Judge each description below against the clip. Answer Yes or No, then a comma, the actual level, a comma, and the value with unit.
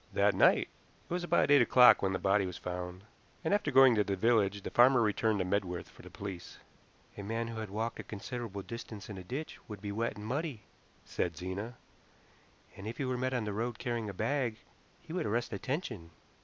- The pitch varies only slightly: No, average, 3.9 semitones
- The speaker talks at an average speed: No, fast, 215 wpm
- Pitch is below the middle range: Yes, low, 110 Hz